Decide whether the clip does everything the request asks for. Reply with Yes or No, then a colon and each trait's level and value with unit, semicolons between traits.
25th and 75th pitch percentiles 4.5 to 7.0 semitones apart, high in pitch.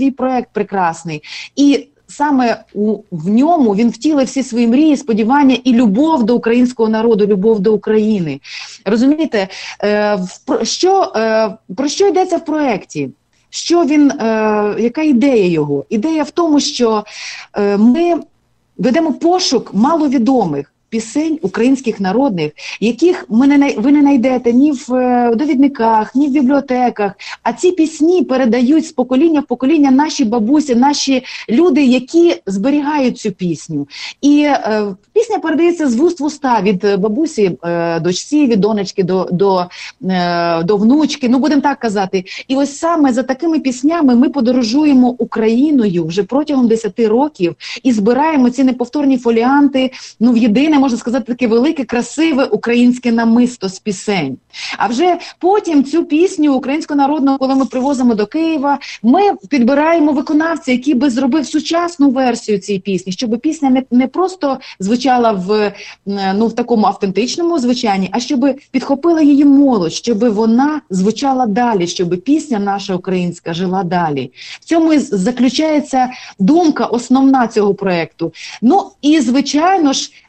Yes: average, 5.1 semitones; very high, 250 Hz